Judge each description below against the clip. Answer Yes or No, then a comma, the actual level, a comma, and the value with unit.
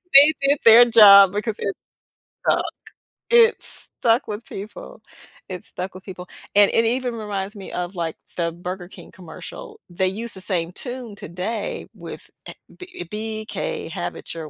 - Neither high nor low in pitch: No, high, 205 Hz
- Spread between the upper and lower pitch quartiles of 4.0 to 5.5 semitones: Yes, average, 4.4 semitones